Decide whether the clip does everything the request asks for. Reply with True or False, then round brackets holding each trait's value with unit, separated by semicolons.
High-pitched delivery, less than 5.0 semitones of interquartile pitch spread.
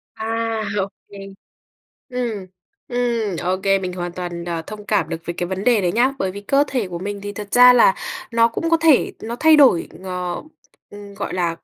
True (205 Hz; 4.5 semitones)